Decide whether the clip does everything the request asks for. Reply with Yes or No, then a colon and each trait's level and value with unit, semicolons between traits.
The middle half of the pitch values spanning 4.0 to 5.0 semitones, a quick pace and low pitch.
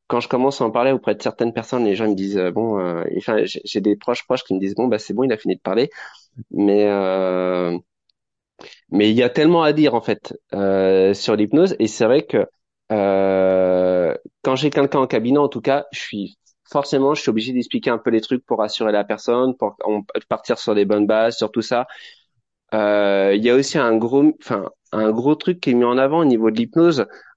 Yes: average, 4.5 semitones; fast, 230 wpm; low, 110 Hz